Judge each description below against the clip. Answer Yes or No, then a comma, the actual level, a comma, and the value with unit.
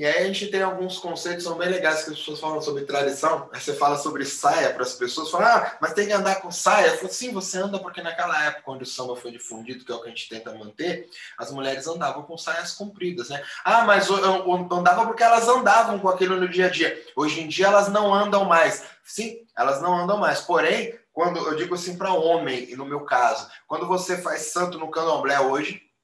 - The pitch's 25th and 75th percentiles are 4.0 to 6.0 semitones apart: Yes, average, 4.4 semitones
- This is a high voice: No, medium, 175 Hz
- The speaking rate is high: Yes, fast, 235 wpm